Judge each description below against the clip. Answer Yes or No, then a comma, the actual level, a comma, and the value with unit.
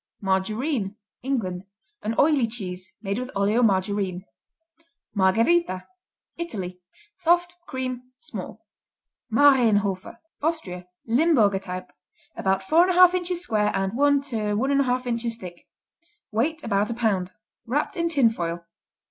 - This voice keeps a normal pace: No, slow, 110 wpm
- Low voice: No, high, 225 Hz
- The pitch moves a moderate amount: No, wide, 6.5 semitones